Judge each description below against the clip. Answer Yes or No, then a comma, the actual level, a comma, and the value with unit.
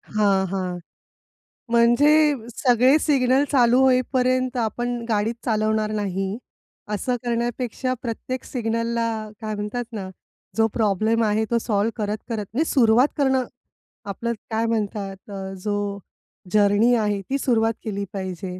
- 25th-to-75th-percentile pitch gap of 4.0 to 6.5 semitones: No, average, 3.0 semitones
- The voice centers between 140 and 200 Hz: No, high, 225 Hz